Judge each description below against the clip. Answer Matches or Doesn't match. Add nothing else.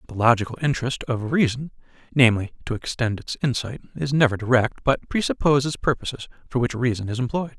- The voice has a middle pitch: Doesn't match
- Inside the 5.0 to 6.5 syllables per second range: Matches